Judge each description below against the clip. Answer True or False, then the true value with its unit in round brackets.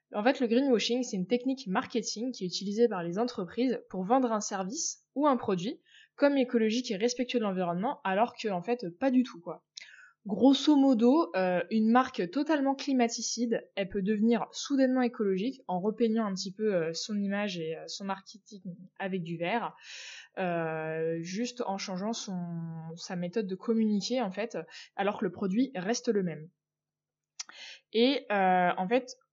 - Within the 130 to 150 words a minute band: False (170 wpm)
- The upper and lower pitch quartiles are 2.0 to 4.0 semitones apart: False (4.6 semitones)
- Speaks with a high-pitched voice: True (220 Hz)